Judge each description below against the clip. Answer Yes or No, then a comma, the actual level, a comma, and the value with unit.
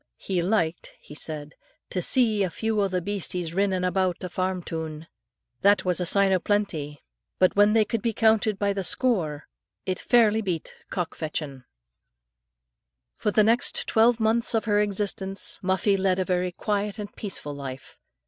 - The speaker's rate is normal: Yes, average, 170 wpm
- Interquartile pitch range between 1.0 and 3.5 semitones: Yes, average, 3.1 semitones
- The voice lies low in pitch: No, high, 190 Hz